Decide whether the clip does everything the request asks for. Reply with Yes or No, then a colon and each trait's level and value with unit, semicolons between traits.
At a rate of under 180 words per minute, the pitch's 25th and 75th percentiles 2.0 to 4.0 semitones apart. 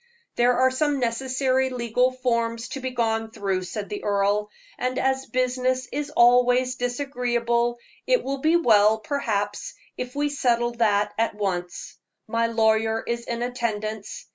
Yes: average, 145 wpm; narrow, 2.5 semitones